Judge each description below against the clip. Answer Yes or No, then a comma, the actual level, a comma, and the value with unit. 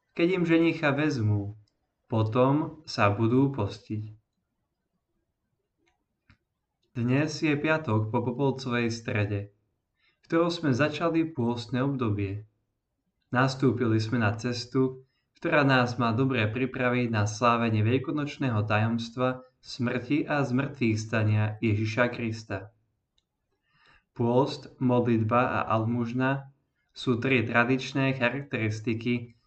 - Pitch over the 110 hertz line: Yes, low, 125 Hz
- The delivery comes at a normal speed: No, slow, 95 wpm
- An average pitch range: Yes, average, 3.3 semitones